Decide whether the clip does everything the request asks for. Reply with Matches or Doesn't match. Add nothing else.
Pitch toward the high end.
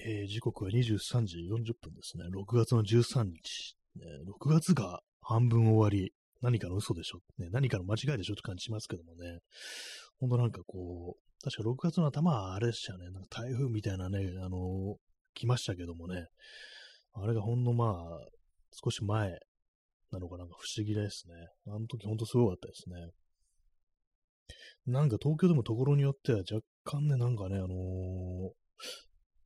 Doesn't match